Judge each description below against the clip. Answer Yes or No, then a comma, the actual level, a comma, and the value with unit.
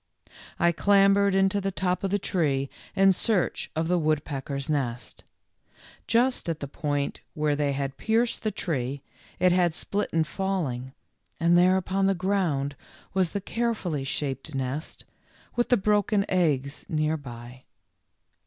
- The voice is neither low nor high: Yes, medium, 170 Hz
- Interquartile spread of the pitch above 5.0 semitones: Yes, wide, 5.6 semitones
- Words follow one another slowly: No, average, 145 wpm